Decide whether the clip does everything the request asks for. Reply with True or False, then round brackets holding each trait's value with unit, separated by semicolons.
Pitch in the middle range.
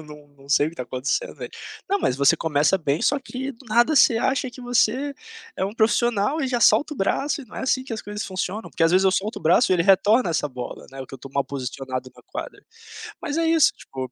False (200 Hz)